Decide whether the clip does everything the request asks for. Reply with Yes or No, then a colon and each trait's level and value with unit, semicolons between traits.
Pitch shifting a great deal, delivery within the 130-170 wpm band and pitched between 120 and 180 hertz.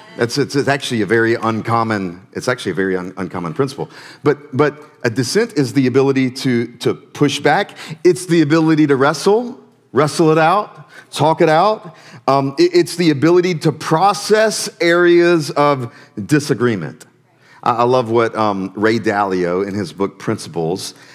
Yes: wide, 6.0 semitones; average, 155 wpm; medium, 140 Hz